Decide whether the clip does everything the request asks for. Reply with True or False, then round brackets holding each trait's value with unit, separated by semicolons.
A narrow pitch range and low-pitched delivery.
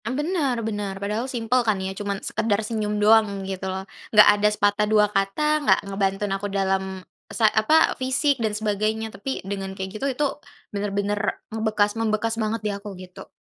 False (2.2 semitones; 210 Hz)